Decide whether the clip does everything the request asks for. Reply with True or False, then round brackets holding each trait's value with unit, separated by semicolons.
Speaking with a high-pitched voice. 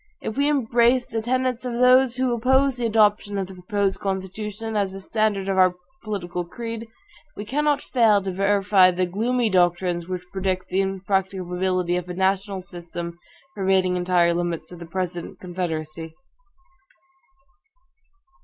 True (195 Hz)